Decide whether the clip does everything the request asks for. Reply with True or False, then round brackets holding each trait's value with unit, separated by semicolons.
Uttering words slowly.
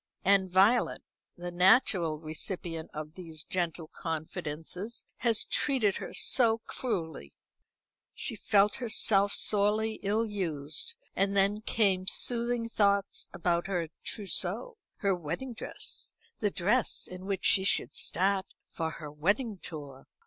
True (125 wpm)